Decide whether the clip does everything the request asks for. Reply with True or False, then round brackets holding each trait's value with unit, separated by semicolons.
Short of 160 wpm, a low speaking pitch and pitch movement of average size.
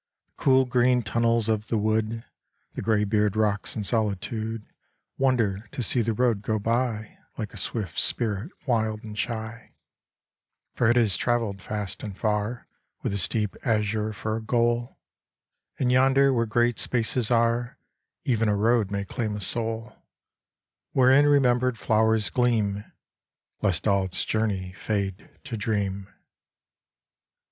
False (140 wpm; 110 Hz; 2.3 semitones)